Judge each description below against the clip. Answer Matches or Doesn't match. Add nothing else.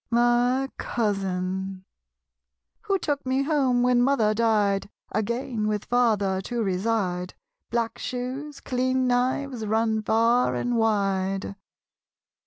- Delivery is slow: Matches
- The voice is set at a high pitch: Matches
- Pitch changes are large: Doesn't match